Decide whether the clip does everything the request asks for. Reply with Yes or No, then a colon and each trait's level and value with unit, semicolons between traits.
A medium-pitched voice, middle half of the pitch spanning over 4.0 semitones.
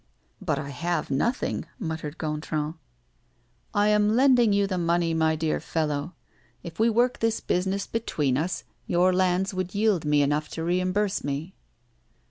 Yes: medium, 175 Hz; average, 4.7 semitones